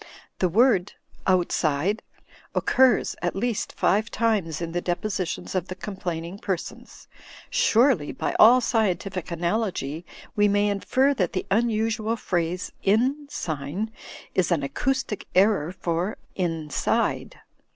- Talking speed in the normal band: No, slow, 120 wpm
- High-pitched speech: Yes, high, 195 Hz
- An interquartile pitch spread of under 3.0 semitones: No, average, 4.3 semitones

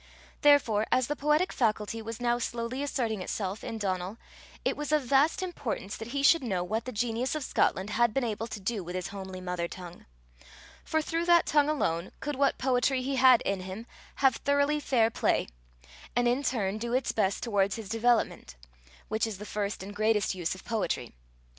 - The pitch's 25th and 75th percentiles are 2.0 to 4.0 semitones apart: No, average, 4.9 semitones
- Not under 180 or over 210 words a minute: Yes, average, 195 wpm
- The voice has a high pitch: Yes, high, 230 Hz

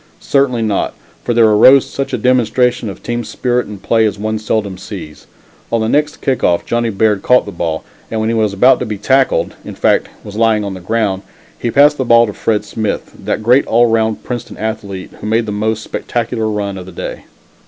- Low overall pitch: Yes, low, 110 Hz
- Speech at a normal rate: No, fast, 215 wpm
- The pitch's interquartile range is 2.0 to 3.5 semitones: Yes, narrow, 2.5 semitones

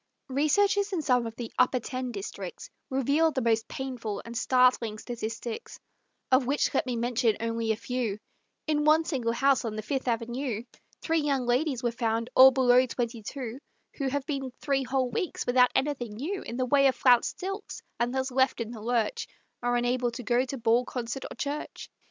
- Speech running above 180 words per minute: Yes, average, 190 wpm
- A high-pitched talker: Yes, very high, 250 Hz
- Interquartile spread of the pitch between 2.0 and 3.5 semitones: Yes, average, 2.7 semitones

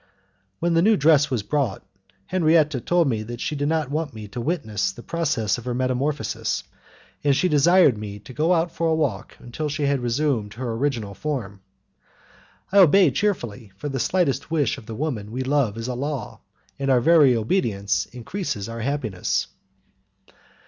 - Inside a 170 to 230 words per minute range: Yes, average, 175 wpm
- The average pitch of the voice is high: No, low, 135 Hz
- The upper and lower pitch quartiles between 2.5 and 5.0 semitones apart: No, wide, 5.5 semitones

